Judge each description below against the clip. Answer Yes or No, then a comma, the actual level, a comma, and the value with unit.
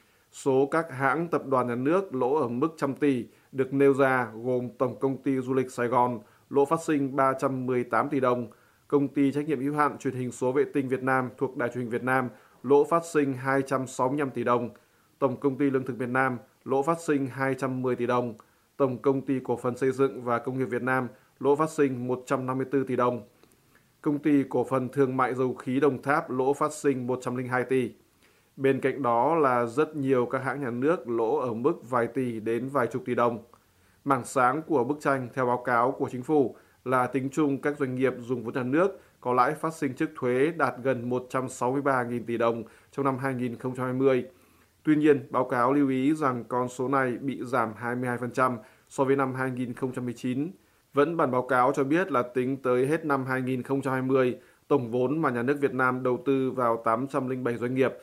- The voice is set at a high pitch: No, low, 130 Hz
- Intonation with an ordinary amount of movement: No, narrow, 2.0 semitones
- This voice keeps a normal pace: Yes, average, 205 wpm